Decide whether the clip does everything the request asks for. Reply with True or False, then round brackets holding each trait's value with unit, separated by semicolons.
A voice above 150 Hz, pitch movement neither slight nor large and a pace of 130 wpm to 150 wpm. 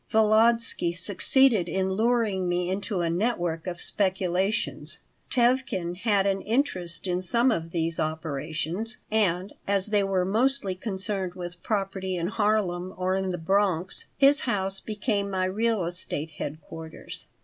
True (190 Hz; 3.6 semitones; 140 wpm)